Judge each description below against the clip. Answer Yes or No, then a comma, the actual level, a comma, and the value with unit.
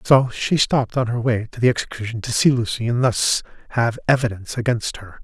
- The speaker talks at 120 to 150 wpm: No, fast, 205 wpm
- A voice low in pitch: Yes, low, 120 Hz